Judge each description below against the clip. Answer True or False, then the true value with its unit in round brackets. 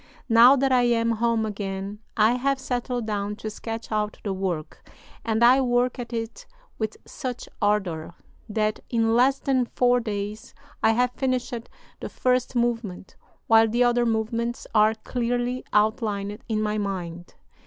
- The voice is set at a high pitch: True (225 Hz)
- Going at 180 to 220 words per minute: False (155 wpm)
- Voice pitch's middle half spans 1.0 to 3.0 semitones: True (2.6 semitones)